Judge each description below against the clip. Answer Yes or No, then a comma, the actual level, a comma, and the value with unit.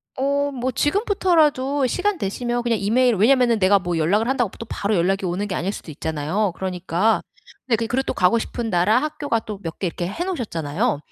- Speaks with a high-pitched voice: Yes, high, 225 Hz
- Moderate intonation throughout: No, wide, 6.0 semitones